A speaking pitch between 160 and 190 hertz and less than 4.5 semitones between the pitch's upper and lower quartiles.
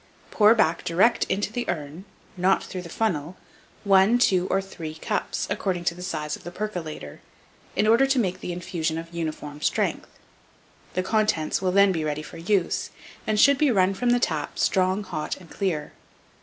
Yes: medium, 185 Hz; average, 4.1 semitones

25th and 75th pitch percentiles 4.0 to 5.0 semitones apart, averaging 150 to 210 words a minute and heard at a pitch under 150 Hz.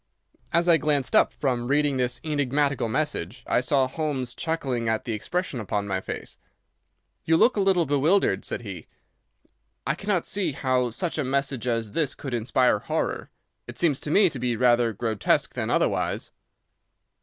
Yes: average, 4.5 semitones; average, 165 wpm; low, 135 Hz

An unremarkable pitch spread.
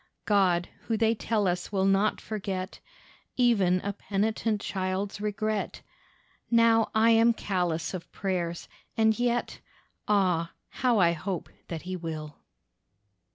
Yes: average, 3.5 semitones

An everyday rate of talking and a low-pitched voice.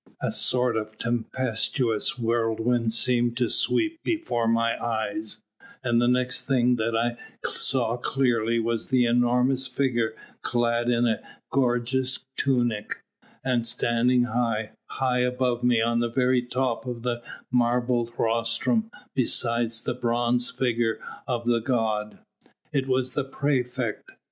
No: slow, 130 wpm; low, 120 Hz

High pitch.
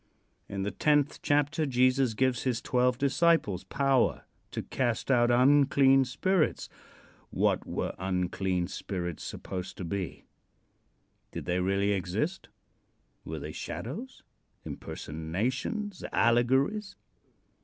No: low, 125 Hz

